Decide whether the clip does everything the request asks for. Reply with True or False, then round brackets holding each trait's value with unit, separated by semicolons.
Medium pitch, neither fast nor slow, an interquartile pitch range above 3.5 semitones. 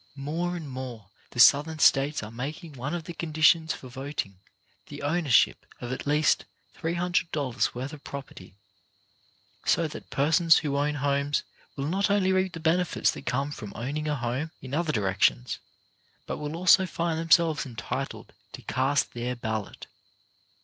True (145 Hz; 160 wpm; 4.1 semitones)